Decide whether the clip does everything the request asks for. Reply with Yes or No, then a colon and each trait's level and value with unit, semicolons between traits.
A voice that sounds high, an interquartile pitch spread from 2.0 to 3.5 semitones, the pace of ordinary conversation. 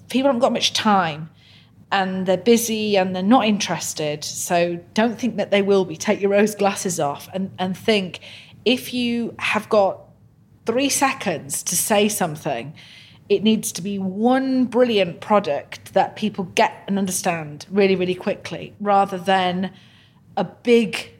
Yes: high, 195 Hz; average, 3.2 semitones; average, 155 wpm